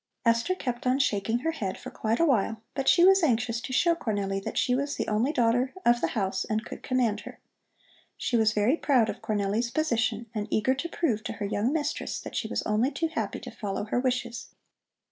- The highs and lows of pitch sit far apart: No, average, 3.9 semitones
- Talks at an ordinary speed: No, fast, 220 wpm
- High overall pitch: Yes, high, 235 Hz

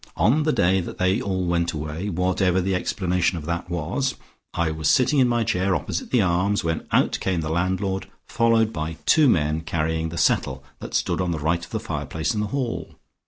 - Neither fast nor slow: No, fast, 210 wpm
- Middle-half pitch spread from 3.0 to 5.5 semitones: Yes, average, 3.9 semitones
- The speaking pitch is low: Yes, very low, 90 Hz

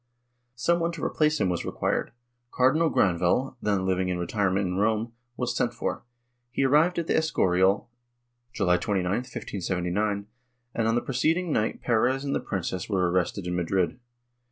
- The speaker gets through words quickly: No, average, 160 wpm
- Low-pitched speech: Yes, low, 105 Hz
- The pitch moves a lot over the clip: Yes, wide, 6.1 semitones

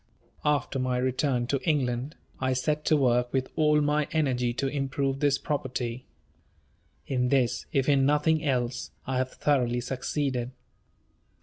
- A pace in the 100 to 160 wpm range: Yes, average, 140 wpm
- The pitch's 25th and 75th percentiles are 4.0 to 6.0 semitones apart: No, average, 2.7 semitones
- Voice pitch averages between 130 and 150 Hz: Yes, low, 135 Hz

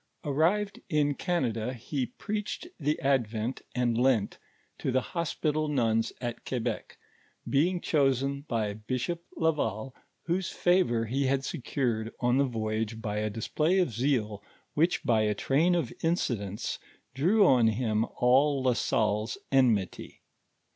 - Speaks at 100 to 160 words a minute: Yes, slow, 135 wpm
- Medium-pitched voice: No, low, 130 Hz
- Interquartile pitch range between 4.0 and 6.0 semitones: Yes, average, 5.2 semitones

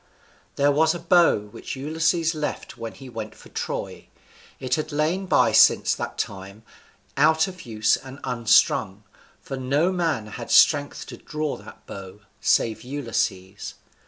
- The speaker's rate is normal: Yes, average, 150 wpm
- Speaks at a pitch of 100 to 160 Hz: Yes, low, 135 Hz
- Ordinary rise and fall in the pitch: No, wide, 6.2 semitones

